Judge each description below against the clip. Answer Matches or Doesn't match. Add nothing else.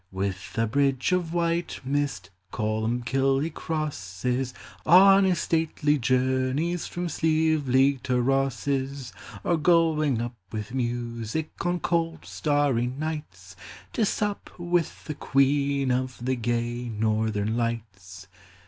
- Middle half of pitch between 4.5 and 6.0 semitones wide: Matches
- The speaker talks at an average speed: Doesn't match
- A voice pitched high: Doesn't match